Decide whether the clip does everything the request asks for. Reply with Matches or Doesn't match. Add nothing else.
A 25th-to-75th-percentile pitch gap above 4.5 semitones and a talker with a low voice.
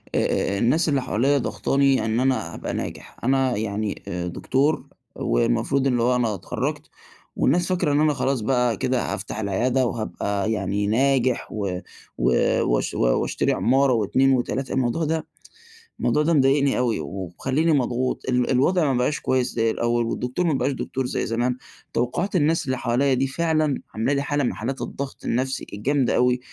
Doesn't match